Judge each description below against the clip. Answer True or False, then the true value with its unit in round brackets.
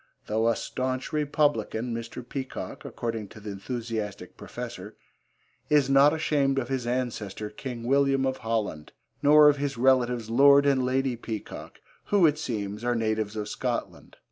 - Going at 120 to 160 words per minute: True (150 wpm)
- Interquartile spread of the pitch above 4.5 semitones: False (3.8 semitones)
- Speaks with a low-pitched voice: True (125 Hz)